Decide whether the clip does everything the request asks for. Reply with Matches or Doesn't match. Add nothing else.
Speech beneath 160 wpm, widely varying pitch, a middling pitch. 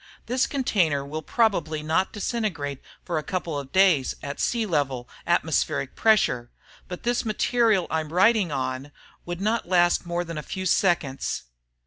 Matches